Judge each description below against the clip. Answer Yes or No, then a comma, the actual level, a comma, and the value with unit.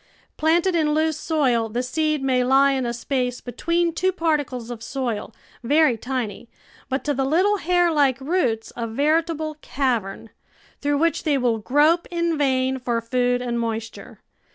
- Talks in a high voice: Yes, very high, 270 Hz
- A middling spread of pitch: Yes, average, 4.4 semitones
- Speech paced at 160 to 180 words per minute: Yes, average, 165 wpm